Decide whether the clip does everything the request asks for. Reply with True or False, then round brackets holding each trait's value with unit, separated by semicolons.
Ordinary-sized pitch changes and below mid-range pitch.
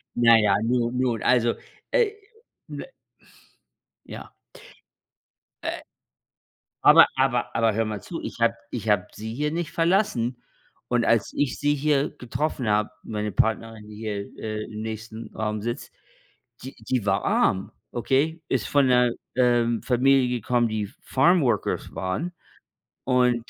True (3.3 semitones; 120 Hz)